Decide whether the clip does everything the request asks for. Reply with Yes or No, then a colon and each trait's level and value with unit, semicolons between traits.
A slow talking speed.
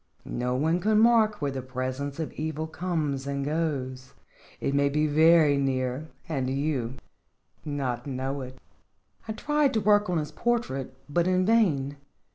No: average, 155 wpm